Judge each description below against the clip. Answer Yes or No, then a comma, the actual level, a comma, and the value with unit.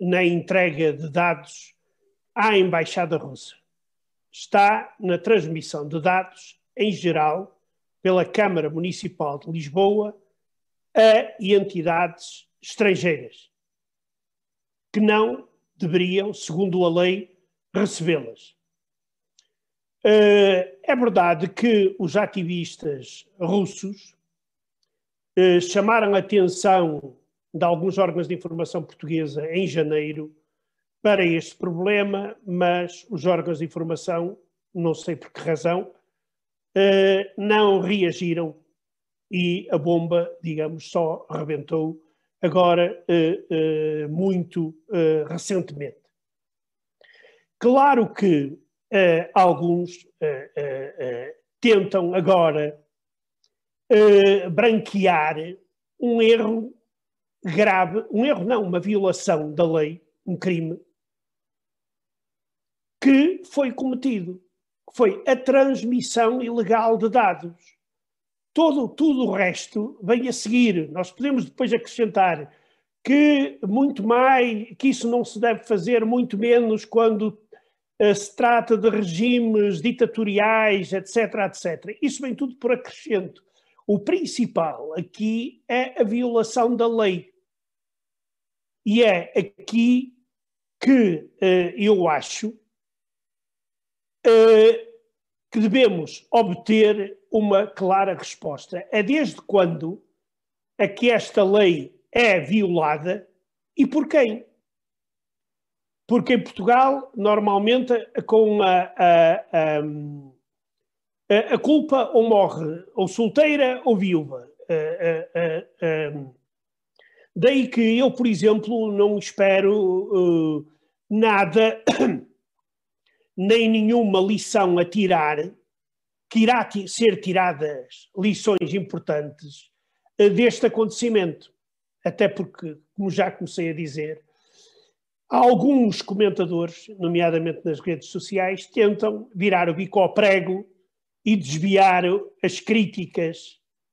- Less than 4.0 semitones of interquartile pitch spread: No, average, 4.9 semitones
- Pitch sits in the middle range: No, high, 195 Hz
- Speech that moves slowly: Yes, slow, 95 wpm